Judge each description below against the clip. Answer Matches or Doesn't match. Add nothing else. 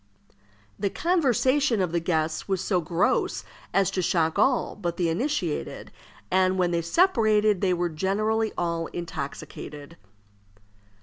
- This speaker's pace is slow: Matches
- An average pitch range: Matches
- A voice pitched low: Doesn't match